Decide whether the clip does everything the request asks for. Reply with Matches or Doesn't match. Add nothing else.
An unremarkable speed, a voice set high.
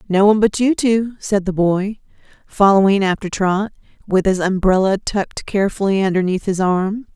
Matches